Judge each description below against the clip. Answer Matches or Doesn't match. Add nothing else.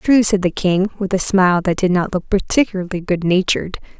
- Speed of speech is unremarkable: Matches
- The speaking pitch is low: Doesn't match